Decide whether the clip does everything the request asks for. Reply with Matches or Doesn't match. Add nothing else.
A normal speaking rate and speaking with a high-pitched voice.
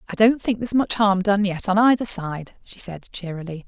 Doesn't match